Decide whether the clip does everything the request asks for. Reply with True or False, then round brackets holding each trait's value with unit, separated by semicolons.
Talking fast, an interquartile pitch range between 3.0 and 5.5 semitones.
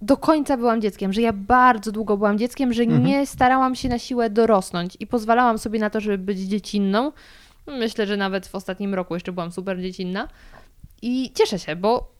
True (190 wpm; 3.8 semitones)